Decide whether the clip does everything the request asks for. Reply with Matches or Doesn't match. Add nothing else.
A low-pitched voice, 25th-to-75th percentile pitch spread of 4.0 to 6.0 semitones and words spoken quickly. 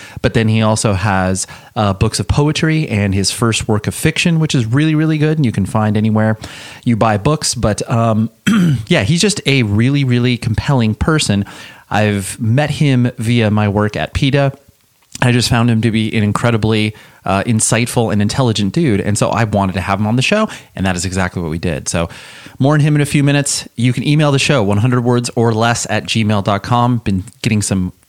Matches